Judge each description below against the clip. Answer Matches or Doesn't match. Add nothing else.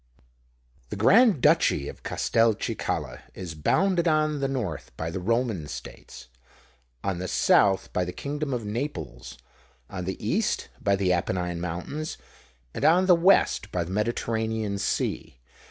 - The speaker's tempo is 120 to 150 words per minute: Matches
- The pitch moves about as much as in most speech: Doesn't match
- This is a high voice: Doesn't match